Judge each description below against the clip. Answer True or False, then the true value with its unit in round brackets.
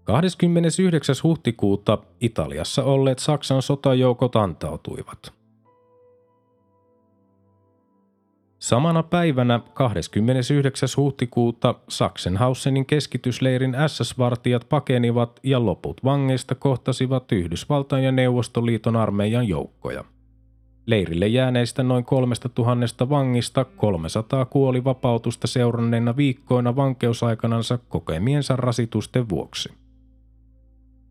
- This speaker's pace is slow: True (75 wpm)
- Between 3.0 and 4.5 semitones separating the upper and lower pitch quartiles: False (2.5 semitones)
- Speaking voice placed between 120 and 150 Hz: True (125 Hz)